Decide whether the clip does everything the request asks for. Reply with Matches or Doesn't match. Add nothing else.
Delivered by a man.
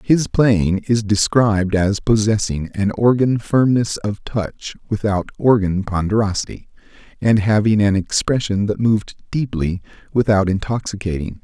Matches